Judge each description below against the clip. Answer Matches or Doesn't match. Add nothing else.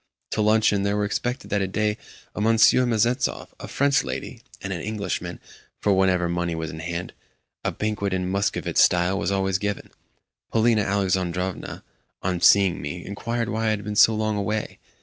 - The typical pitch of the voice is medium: Doesn't match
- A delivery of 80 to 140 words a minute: Doesn't match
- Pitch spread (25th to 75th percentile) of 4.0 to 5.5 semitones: Doesn't match